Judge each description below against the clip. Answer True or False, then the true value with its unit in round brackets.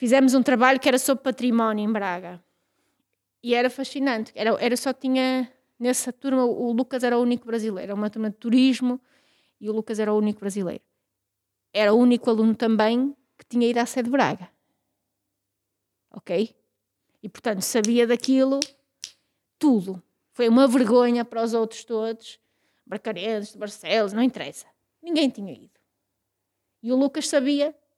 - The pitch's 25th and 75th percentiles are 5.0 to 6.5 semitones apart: False (3.4 semitones)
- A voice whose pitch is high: True (240 Hz)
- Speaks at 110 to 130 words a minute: False (155 wpm)